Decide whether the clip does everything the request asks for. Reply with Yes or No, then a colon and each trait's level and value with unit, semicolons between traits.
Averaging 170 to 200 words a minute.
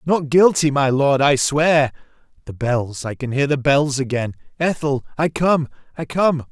Yes: average, 175 wpm